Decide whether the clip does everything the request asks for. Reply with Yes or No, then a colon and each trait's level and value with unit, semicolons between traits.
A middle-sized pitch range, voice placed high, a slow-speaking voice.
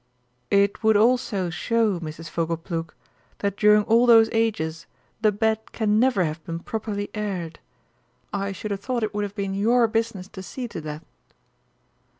No: average, 4.2 semitones; high, 205 Hz; average, 160 wpm